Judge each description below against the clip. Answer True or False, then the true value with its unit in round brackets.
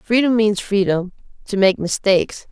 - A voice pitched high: True (205 Hz)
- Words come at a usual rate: True (145 wpm)